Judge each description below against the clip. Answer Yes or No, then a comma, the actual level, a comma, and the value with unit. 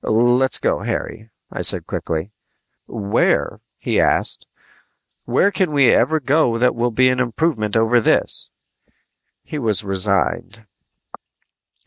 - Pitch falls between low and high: No, low, 115 Hz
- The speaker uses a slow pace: Yes, slow, 120 wpm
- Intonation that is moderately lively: Yes, average, 3.5 semitones